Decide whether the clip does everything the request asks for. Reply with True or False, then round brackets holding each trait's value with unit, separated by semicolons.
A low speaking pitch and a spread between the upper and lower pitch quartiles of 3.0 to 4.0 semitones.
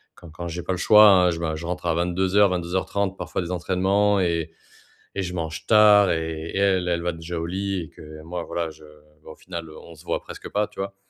False (90 Hz; 2.6 semitones)